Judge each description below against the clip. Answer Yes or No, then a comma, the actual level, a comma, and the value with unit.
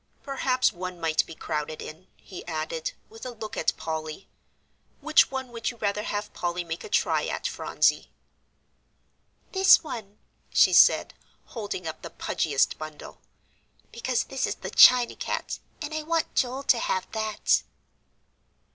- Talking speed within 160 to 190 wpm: No, average, 150 wpm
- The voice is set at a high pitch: Yes, high, 210 Hz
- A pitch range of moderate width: No, wide, 7.6 semitones